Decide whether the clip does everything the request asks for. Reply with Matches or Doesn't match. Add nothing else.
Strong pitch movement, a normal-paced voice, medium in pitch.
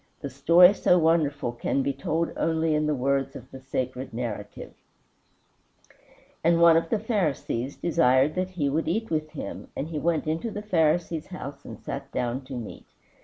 Doesn't match